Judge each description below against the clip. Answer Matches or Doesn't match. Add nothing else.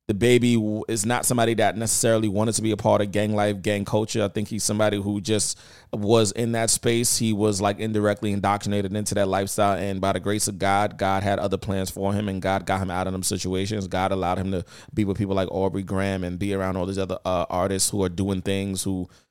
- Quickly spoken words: Matches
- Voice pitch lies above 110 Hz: Doesn't match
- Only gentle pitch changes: Matches